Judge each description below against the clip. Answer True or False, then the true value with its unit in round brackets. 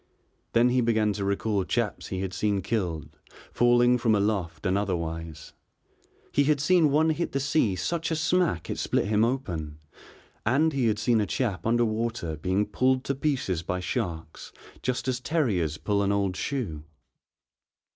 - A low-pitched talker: True (110 Hz)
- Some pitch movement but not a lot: False (5.7 semitones)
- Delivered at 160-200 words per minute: True (165 wpm)